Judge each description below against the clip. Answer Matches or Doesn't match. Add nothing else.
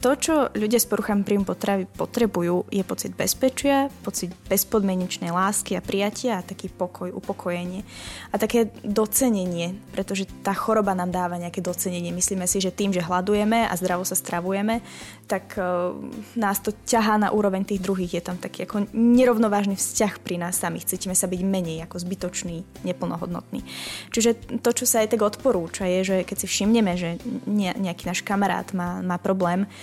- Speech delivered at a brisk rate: Matches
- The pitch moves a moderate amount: Matches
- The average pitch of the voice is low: Doesn't match